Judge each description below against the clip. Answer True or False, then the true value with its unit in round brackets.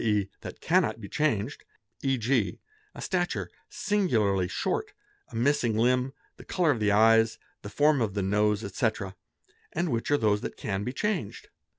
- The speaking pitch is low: True (115 Hz)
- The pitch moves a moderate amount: False (5.8 semitones)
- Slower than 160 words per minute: False (165 wpm)